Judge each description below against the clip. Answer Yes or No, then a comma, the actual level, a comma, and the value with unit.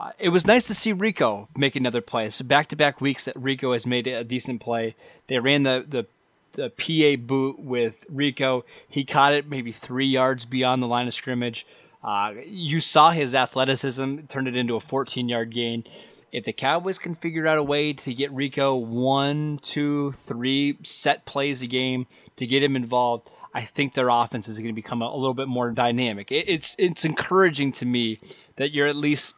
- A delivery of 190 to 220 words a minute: Yes, average, 200 wpm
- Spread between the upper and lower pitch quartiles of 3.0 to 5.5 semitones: No, narrow, 2.6 semitones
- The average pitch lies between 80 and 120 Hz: No, low, 135 Hz